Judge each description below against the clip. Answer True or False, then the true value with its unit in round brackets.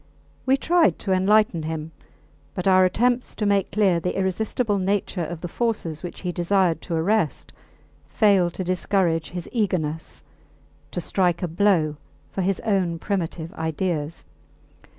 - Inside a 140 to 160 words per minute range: True (145 wpm)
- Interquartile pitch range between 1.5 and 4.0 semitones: True (3.5 semitones)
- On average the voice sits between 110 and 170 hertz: False (185 Hz)